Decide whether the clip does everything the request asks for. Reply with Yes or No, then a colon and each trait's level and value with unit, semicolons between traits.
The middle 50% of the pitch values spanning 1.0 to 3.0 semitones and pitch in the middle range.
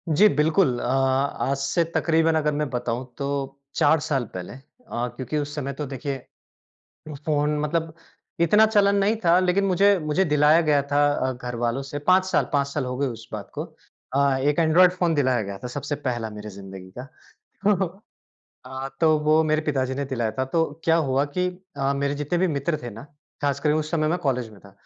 No: average, 3.7 semitones; medium, 145 Hz